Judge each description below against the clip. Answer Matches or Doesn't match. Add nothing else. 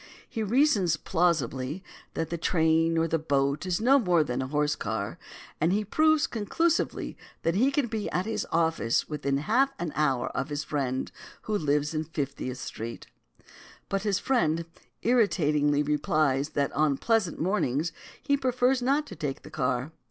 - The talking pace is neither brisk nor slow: Matches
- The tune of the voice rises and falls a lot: Matches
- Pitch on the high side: Doesn't match